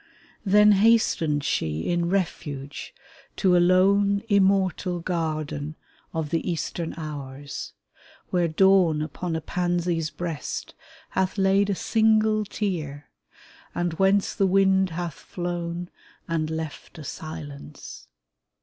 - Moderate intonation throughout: Yes, average, 3.6 semitones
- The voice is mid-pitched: Yes, medium, 175 Hz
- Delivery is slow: Yes, slow, 115 wpm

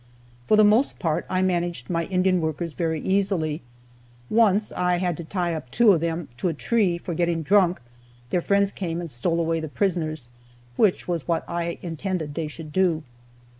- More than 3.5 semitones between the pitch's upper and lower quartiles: No, narrow, 2.6 semitones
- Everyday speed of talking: Yes, average, 185 wpm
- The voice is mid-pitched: Yes, medium, 175 Hz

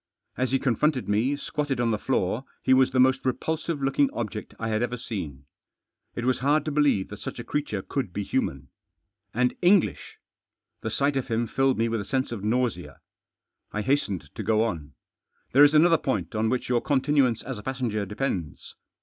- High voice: No, low, 125 Hz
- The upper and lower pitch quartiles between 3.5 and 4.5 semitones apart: Yes, average, 4.1 semitones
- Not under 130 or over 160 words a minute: No, average, 195 wpm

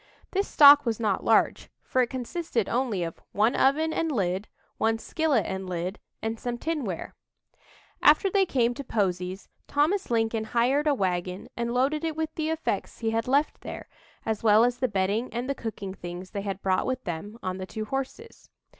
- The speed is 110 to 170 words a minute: No, average, 190 wpm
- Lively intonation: Yes, wide, 6.0 semitones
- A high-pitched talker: Yes, high, 230 Hz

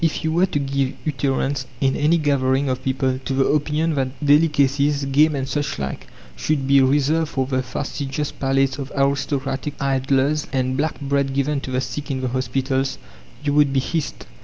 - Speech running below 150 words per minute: No, average, 185 wpm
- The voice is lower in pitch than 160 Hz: Yes, medium, 140 Hz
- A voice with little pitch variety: Yes, narrow, 1.7 semitones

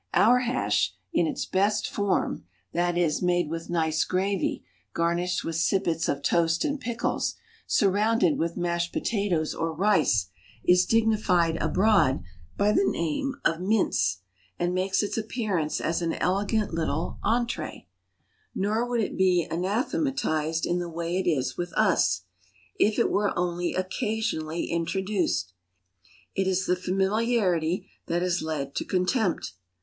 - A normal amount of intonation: Yes, average, 3.8 semitones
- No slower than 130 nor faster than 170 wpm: Yes, average, 140 wpm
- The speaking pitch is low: No, medium, 180 Hz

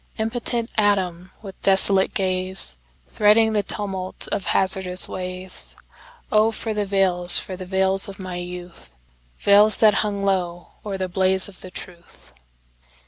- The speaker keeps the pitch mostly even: Yes, narrow, 2.2 semitones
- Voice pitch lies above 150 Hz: Yes, high, 190 Hz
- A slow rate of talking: Yes, slow, 130 wpm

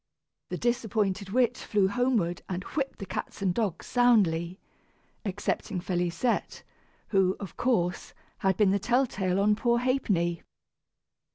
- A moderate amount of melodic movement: Yes, average, 4.7 semitones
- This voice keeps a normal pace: No, slow, 130 wpm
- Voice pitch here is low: No, high, 200 Hz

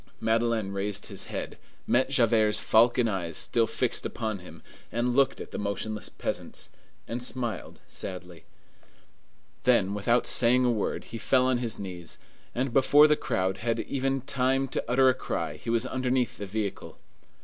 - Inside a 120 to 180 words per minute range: Yes, average, 160 wpm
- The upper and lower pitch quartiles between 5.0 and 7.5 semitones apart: No, average, 3.7 semitones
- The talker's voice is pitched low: Yes, low, 115 Hz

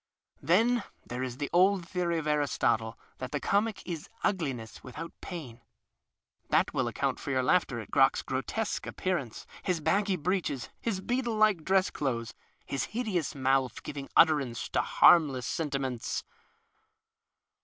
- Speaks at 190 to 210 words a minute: No, average, 145 wpm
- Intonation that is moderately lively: No, wide, 6.2 semitones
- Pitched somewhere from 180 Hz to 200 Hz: No, medium, 155 Hz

